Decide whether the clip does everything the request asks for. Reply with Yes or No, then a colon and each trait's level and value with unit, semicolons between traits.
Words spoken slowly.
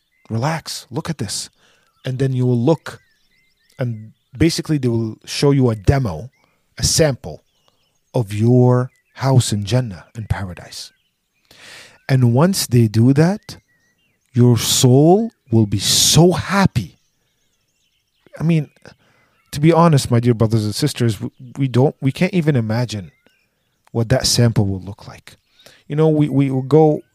No: average, 145 wpm